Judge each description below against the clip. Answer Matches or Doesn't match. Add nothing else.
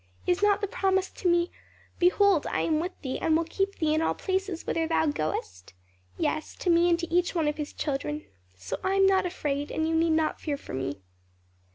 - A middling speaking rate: Doesn't match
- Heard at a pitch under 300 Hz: Doesn't match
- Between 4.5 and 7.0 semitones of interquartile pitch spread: Doesn't match